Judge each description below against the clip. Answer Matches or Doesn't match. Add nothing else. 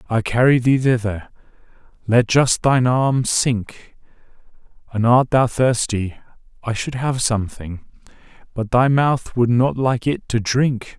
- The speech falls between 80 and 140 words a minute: Matches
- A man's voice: Matches